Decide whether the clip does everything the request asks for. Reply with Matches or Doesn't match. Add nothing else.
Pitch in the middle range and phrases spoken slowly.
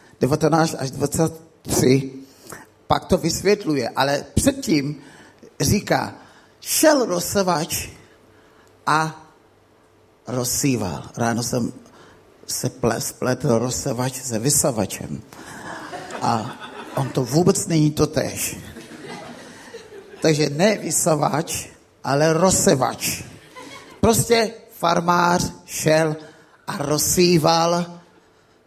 Matches